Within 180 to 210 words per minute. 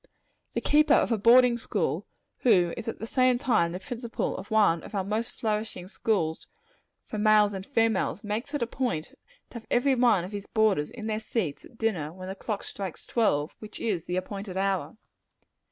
Yes: average, 200 wpm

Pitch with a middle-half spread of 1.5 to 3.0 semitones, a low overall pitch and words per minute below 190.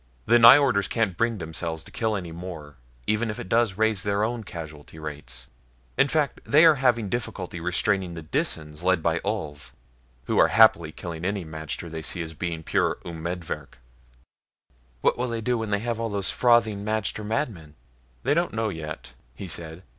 No: wide, 5.6 semitones; very low, 95 Hz; average, 180 wpm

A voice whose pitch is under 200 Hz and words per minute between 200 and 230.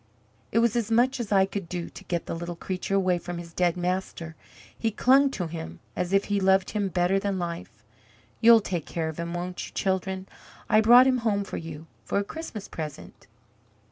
Yes: high, 190 Hz; fast, 205 wpm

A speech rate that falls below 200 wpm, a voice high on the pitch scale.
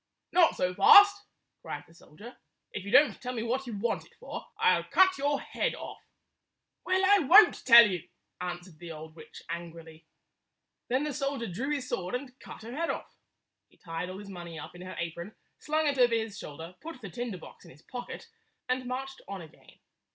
No: fast, 205 wpm; high, 230 Hz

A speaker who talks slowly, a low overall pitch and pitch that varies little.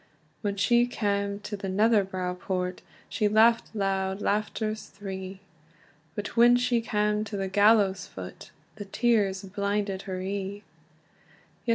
No: slow, 130 wpm; high, 200 Hz; narrow, 1.9 semitones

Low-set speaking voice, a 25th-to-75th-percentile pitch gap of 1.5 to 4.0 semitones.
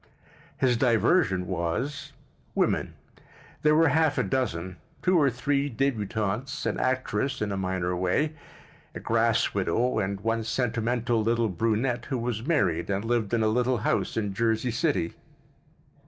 No: low, 115 Hz; average, 4.6 semitones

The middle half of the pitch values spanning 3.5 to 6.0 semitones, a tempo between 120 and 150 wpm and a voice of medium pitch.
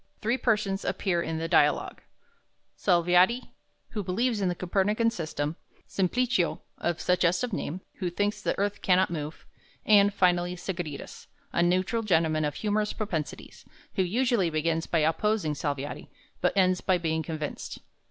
Yes: average, 3.9 semitones; average, 145 wpm; medium, 180 Hz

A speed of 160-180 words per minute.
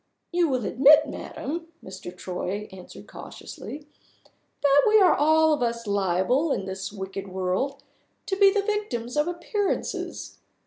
No: average, 140 wpm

